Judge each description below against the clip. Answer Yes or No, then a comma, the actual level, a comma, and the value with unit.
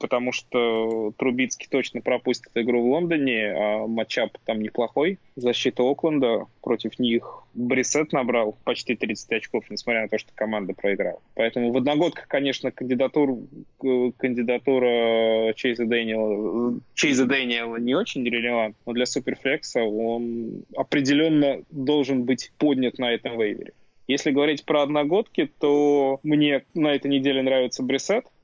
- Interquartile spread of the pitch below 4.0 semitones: Yes, average, 2.9 semitones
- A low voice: Yes, low, 125 Hz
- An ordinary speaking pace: Yes, average, 130 wpm